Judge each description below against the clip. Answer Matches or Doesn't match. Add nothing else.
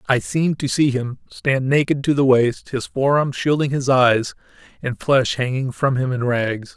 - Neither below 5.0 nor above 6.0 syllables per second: Doesn't match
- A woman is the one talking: Doesn't match